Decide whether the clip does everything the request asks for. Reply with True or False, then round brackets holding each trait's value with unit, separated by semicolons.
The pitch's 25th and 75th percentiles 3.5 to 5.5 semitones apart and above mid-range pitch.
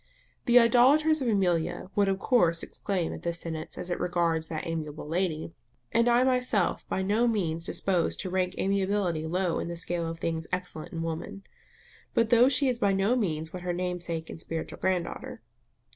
False (3.9 semitones; 180 Hz)